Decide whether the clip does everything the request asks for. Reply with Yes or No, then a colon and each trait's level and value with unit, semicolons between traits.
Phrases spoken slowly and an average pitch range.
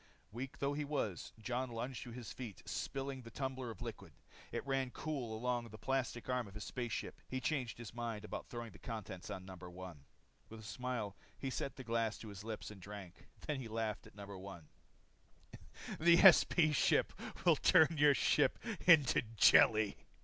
No: average, 185 wpm; average, 4.0 semitones